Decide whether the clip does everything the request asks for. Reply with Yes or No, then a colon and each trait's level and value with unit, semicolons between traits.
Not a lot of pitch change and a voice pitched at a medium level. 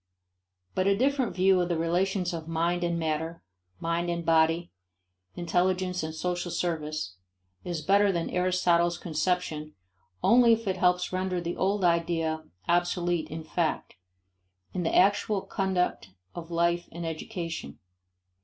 Yes: narrow, 1.9 semitones; medium, 175 Hz